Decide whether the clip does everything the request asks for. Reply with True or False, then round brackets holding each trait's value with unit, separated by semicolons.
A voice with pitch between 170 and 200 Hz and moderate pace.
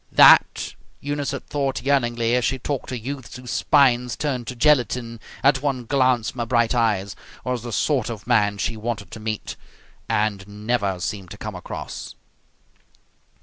False (120 Hz; 165 wpm)